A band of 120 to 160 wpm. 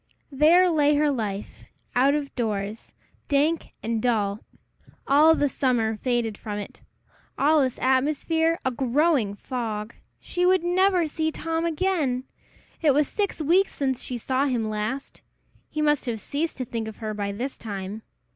Yes: average, 155 wpm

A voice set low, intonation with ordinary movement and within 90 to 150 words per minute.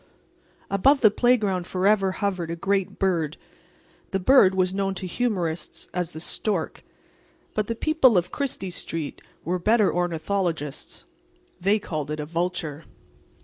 No: medium, 185 Hz; average, 3.3 semitones; average, 140 wpm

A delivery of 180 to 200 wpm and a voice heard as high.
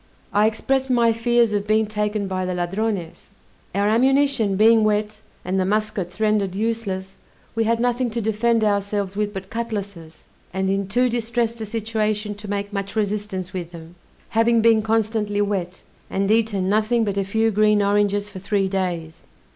No: average, 170 wpm; high, 210 Hz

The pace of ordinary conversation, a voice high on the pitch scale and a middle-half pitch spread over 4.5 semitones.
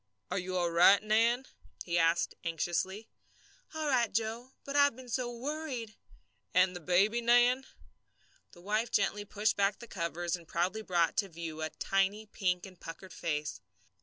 Yes: average, 165 wpm; high, 200 Hz; average, 5.1 semitones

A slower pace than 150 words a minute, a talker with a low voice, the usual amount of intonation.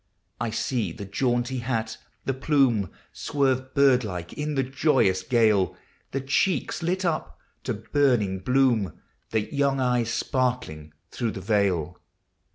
Yes: average, 140 wpm; low, 120 Hz; average, 4.6 semitones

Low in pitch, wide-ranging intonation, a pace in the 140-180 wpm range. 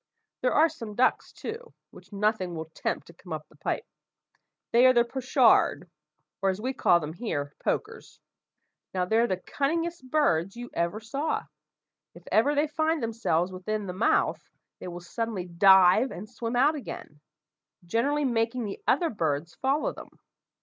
No: high, 225 Hz; wide, 6.5 semitones; average, 165 wpm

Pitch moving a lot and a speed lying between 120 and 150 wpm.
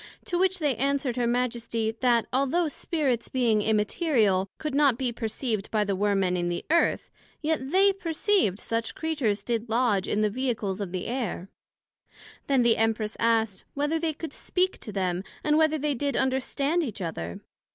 No: wide, 5.7 semitones; average, 180 wpm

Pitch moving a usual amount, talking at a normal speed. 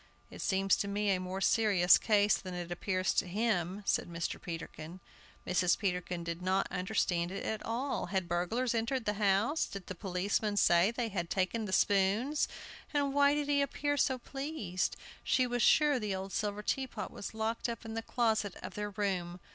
Yes: average, 4.0 semitones; average, 185 wpm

